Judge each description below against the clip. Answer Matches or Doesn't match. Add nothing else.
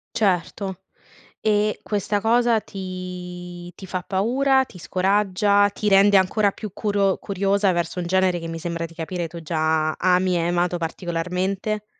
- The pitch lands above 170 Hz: Matches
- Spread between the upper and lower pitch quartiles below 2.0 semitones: Doesn't match